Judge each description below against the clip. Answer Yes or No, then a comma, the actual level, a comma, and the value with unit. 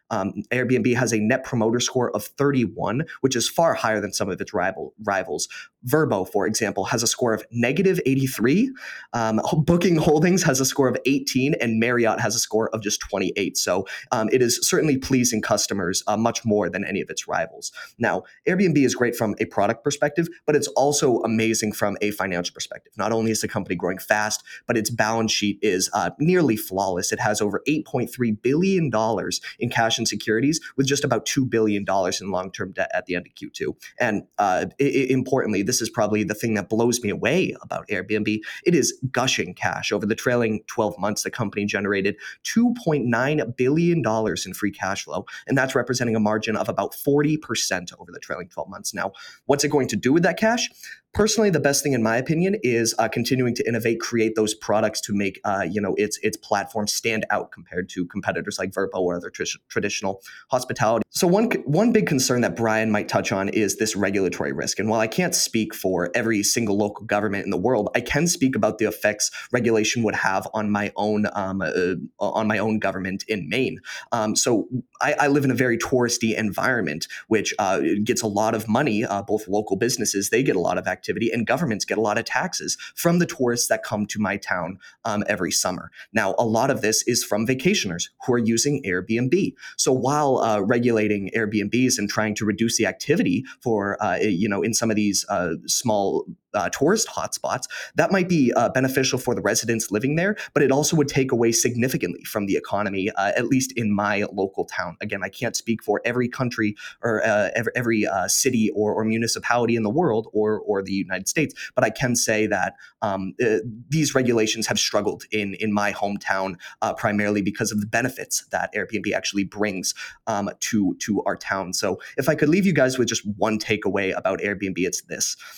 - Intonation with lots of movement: No, average, 3.9 semitones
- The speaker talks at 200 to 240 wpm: Yes, fast, 205 wpm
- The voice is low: Yes, low, 115 Hz